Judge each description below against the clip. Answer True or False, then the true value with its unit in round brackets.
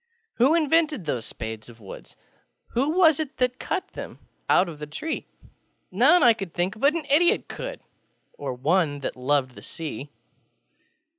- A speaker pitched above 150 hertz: True (190 Hz)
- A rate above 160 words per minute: False (150 wpm)